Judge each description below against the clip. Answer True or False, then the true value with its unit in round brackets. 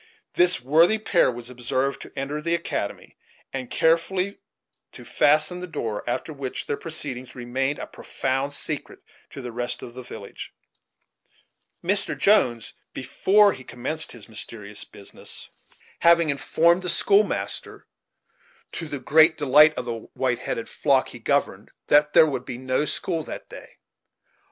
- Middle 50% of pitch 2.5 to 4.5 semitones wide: False (5.0 semitones)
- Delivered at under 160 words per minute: True (150 wpm)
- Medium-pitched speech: True (145 Hz)